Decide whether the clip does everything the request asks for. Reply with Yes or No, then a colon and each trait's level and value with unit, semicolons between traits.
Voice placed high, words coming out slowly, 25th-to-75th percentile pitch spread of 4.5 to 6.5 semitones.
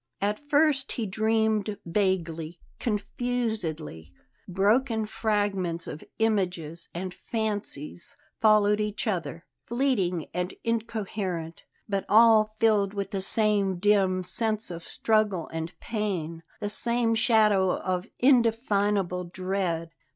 No: high, 205 Hz; slow, 105 wpm; average, 3.6 semitones